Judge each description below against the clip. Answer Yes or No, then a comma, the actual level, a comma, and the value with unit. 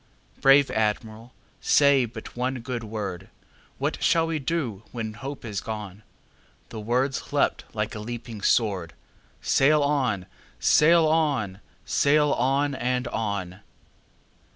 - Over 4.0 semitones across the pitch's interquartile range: Yes, average, 4.8 semitones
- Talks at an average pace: No, slow, 110 wpm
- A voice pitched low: Yes, low, 120 Hz